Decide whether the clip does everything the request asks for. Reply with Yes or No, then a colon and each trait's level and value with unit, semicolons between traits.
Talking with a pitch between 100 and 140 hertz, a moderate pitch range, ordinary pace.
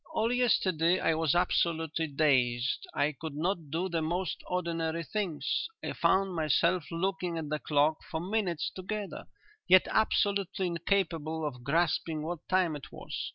No: medium, 165 Hz; average, 3.1 semitones; average, 150 wpm